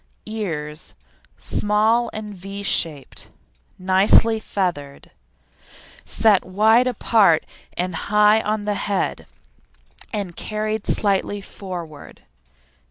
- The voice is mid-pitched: No, high, 205 Hz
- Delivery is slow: Yes, slow, 90 wpm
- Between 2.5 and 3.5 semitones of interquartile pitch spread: Yes, average, 2.9 semitones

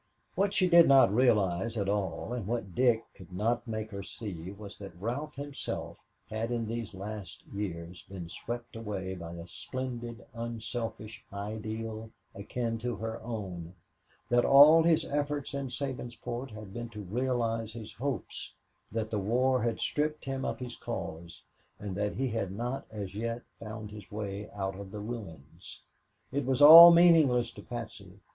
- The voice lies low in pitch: Yes, low, 115 Hz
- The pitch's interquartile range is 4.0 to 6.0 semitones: No, average, 3.6 semitones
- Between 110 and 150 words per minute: No, average, 165 wpm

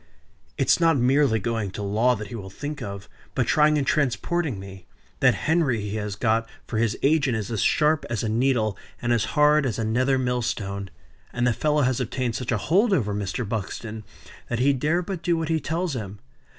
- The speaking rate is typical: No, fast, 210 wpm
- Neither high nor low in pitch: No, low, 120 Hz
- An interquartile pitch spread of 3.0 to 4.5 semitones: No, wide, 5.4 semitones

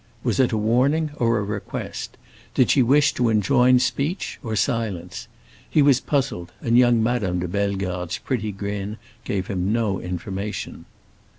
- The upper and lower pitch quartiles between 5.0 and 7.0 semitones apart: No, average, 4.1 semitones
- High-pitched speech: No, low, 110 Hz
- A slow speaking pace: No, average, 155 wpm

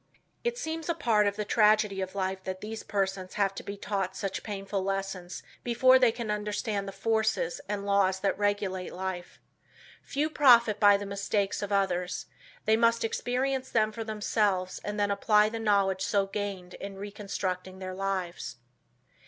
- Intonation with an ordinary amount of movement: No, narrow, 2.1 semitones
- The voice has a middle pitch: No, high, 205 Hz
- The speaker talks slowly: No, average, 170 wpm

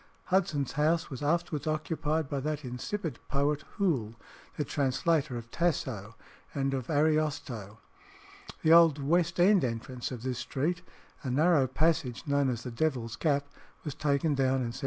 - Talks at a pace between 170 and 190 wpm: No, average, 155 wpm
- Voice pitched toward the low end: No, medium, 145 Hz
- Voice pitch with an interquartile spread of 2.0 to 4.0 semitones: Yes, average, 3.6 semitones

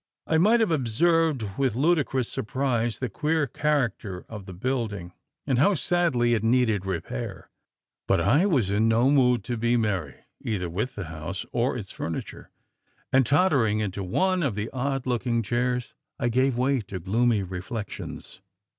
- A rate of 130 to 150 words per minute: No, average, 160 wpm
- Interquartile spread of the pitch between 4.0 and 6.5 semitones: Yes, average, 4.7 semitones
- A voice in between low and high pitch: No, low, 120 Hz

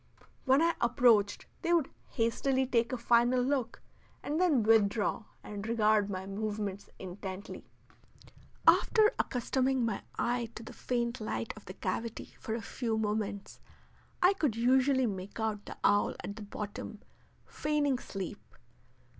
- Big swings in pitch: No, average, 3.8 semitones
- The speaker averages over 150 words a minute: No, average, 140 wpm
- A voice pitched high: Yes, high, 230 Hz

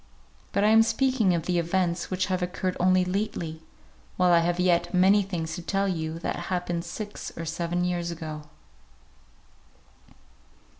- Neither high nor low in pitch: Yes, medium, 180 Hz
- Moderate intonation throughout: No, narrow, 1.8 semitones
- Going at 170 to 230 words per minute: No, average, 155 wpm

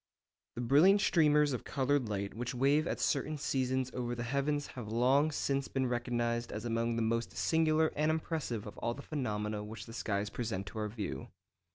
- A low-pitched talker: Yes, low, 125 Hz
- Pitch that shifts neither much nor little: Yes, average, 4.0 semitones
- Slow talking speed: No, average, 195 wpm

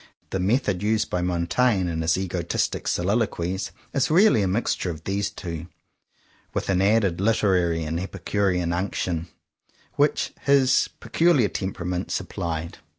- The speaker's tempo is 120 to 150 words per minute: Yes, average, 140 wpm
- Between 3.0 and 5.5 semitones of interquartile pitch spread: Yes, average, 3.5 semitones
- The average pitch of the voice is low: Yes, very low, 95 Hz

